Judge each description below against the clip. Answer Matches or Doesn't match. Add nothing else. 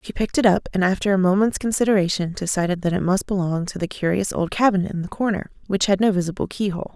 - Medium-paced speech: Doesn't match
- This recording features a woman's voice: Matches